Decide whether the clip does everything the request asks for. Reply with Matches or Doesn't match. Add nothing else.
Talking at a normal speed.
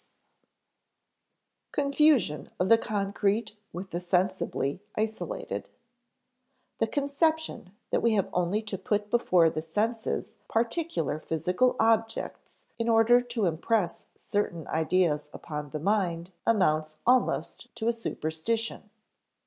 Doesn't match